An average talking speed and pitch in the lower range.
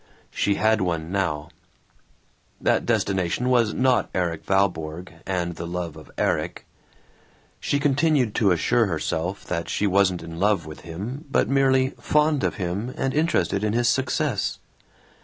Yes: average, 145 wpm; low, 100 Hz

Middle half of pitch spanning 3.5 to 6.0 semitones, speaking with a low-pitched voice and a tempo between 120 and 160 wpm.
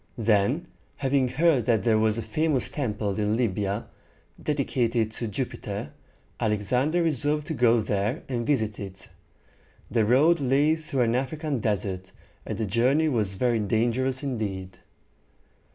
Yes: average, 4.5 semitones; low, 120 Hz; average, 140 wpm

